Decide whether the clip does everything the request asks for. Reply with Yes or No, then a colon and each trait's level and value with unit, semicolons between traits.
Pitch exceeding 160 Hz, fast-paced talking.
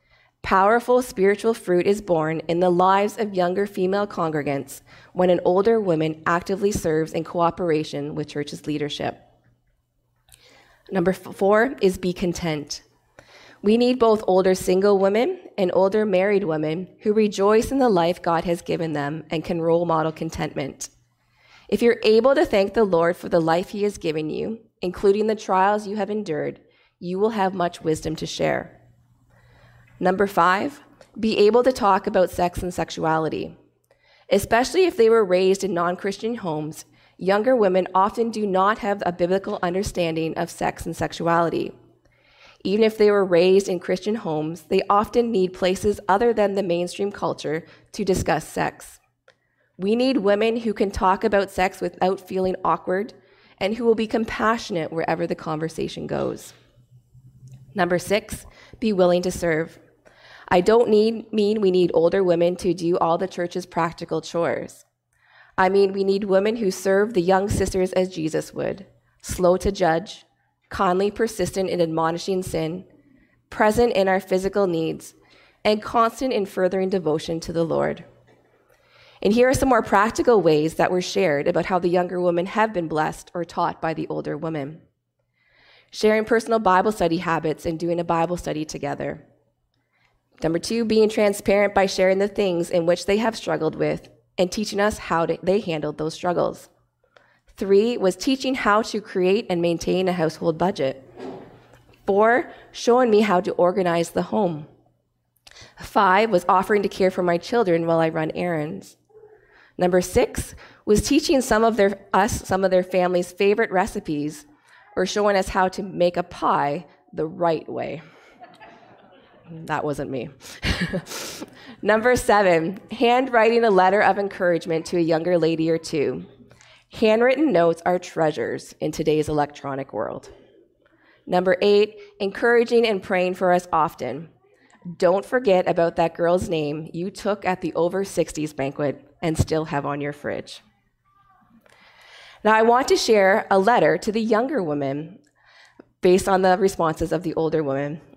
No: medium, 185 Hz; average, 160 wpm